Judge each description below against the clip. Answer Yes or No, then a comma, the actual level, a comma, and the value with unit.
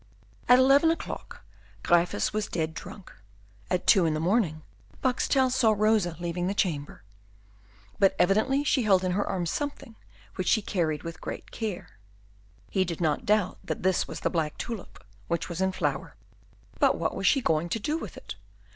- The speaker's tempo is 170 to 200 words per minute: Yes, average, 175 wpm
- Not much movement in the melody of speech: No, average, 4.9 semitones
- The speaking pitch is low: No, high, 190 Hz